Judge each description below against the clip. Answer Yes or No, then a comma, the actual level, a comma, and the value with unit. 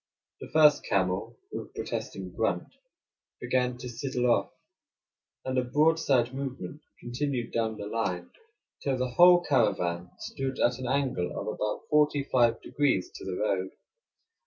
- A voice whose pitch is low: Yes, low, 125 Hz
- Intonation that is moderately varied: Yes, average, 4.5 semitones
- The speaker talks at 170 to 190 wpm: No, average, 145 wpm